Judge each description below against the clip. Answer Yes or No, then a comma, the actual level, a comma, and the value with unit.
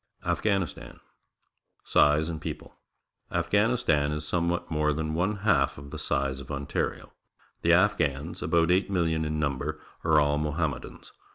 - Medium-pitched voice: No, very low, 80 Hz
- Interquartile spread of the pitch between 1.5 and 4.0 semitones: Yes, average, 2.8 semitones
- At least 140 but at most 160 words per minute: Yes, average, 155 wpm